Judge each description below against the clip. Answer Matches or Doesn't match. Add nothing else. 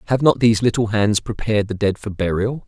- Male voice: Matches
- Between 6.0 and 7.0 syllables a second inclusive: Matches